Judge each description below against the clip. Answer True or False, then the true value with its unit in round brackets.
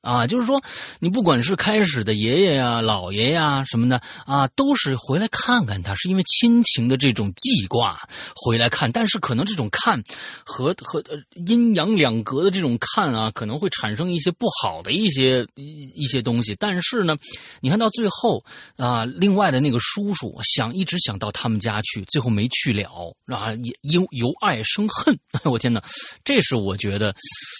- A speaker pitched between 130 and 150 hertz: True (135 Hz)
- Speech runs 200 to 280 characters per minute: True (265 characters per minute)